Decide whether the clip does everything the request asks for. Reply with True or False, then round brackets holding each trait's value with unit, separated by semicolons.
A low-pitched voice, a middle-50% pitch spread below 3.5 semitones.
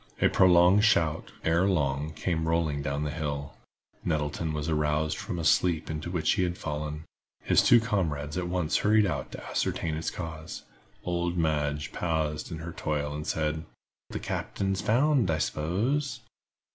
True (80 Hz; 2.8 semitones)